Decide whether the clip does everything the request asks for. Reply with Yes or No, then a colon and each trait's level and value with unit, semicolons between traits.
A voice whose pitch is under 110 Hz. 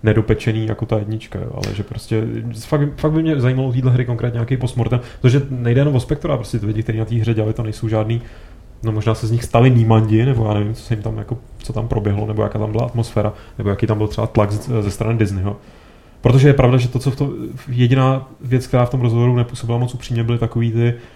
No: low, 115 Hz